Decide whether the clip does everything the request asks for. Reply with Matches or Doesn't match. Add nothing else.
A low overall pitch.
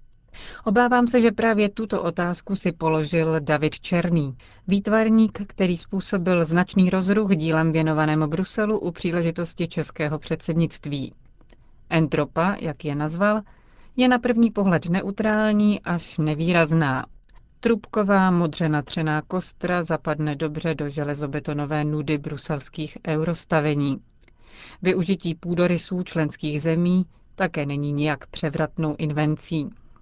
Doesn't match